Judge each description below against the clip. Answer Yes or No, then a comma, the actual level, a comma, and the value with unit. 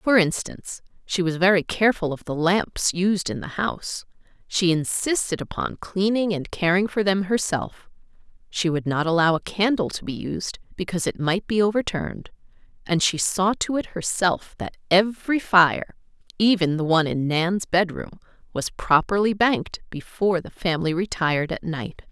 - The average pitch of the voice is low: No, medium, 185 Hz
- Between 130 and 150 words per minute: No, average, 160 wpm